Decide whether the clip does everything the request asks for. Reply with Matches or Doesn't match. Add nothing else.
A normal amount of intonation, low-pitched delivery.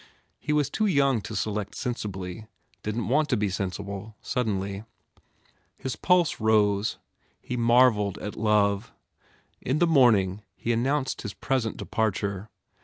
Matches